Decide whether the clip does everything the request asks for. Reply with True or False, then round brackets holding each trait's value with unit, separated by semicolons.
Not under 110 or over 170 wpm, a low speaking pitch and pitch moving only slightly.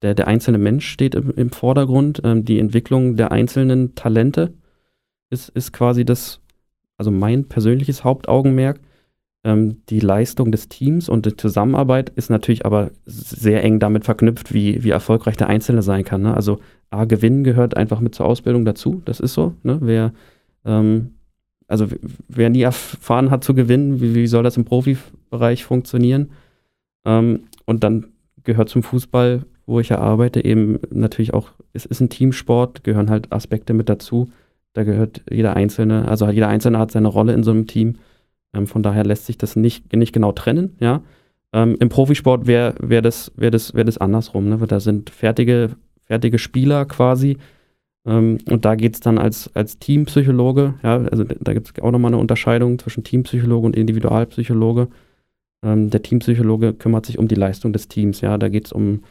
False (180 wpm; 115 Hz; 2.2 semitones)